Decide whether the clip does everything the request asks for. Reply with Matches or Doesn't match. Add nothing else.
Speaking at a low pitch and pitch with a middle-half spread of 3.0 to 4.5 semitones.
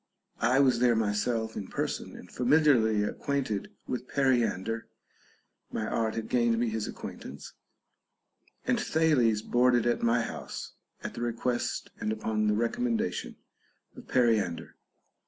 Doesn't match